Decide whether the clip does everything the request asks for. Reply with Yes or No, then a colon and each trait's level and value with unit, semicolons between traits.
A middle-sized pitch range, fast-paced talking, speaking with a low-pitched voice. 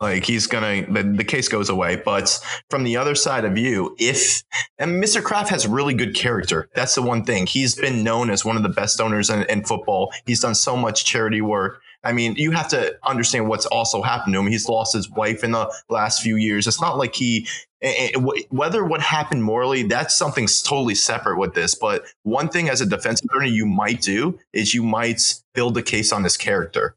Yes: average, 3.3 semitones; fast, 220 wpm; low, 115 Hz